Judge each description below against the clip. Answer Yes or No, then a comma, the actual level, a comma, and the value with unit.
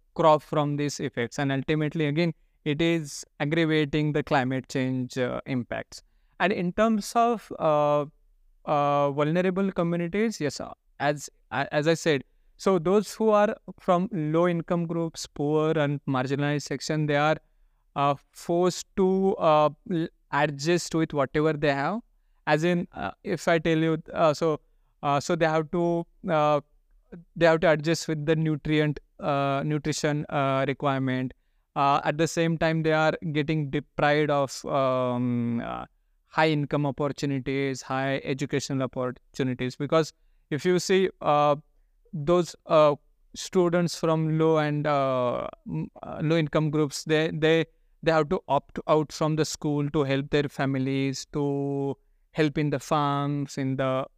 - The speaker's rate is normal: Yes, average, 145 wpm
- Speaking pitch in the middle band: Yes, medium, 150 Hz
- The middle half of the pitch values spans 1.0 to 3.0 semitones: Yes, average, 2.7 semitones